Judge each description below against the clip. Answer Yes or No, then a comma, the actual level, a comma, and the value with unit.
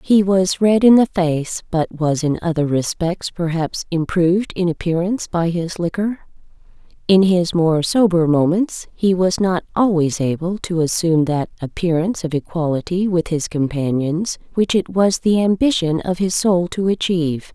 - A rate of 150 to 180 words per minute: Yes, average, 160 wpm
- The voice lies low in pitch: No, medium, 175 Hz